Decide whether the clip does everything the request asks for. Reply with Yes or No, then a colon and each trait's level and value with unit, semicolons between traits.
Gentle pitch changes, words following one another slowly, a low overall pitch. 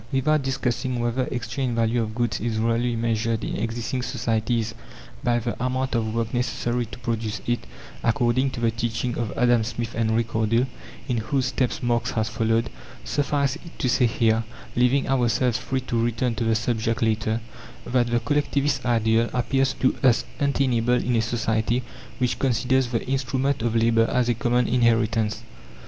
No: narrow, 1.9 semitones; average, 165 wpm; low, 120 Hz